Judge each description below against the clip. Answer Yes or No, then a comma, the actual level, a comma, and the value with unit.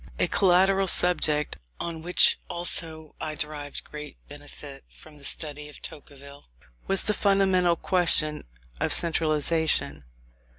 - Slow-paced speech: Yes, slow, 120 wpm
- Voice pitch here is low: No, medium, 155 Hz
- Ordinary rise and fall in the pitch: Yes, average, 3.2 semitones